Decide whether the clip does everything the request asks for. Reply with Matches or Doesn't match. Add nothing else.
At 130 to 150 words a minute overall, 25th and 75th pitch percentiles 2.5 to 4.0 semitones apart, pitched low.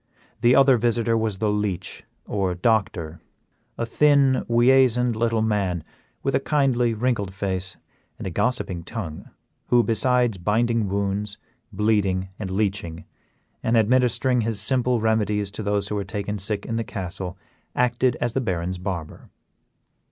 Matches